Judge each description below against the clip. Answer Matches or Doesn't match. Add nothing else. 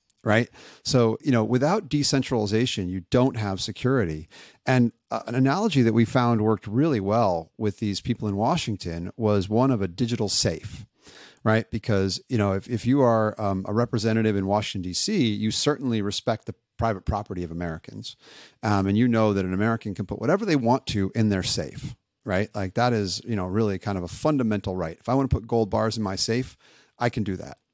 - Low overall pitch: Matches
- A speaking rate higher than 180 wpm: Matches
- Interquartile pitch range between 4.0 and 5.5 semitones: Doesn't match